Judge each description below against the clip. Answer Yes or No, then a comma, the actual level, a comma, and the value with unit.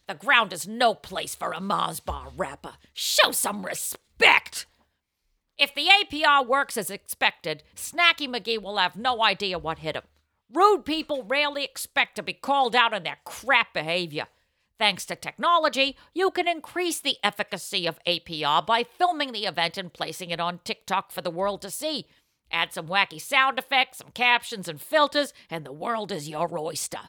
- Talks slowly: No, average, 175 wpm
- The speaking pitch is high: Yes, high, 220 Hz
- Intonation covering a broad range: Yes, wide, 8.0 semitones